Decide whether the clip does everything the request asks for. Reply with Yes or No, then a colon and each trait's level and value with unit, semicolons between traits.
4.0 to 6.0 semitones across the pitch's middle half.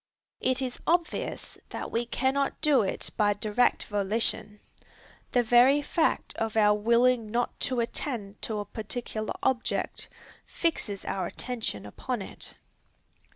No: average, 3.5 semitones